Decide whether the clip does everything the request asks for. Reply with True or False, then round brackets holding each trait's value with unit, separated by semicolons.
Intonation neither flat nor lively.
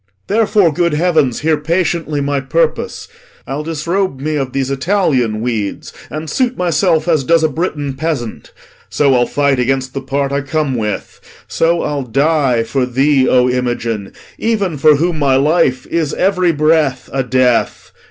True (3.8 semitones)